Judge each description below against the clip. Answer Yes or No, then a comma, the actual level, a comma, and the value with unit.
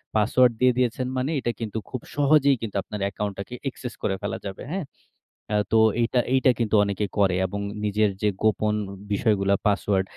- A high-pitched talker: No, low, 110 Hz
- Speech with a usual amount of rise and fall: Yes, average, 3.8 semitones